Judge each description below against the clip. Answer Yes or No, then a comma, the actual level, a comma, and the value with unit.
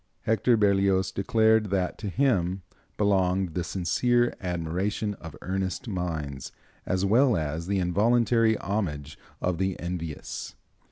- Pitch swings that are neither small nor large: Yes, average, 3.4 semitones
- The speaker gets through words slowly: Yes, slow, 120 wpm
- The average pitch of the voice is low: Yes, very low, 95 Hz